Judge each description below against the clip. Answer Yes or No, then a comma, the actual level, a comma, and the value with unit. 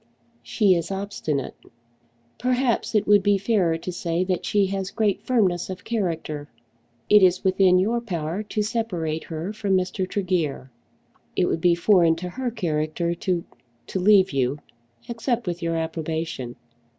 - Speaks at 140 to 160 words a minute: Yes, average, 150 wpm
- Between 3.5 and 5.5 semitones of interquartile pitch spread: Yes, average, 3.8 semitones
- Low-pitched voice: No, medium, 185 Hz